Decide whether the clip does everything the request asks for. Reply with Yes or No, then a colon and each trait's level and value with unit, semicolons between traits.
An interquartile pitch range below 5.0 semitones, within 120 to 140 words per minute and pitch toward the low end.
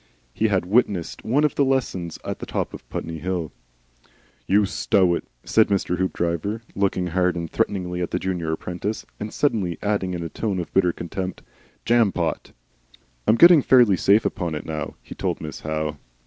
No: average, 3.7 semitones; average, 175 wpm; very low, 95 Hz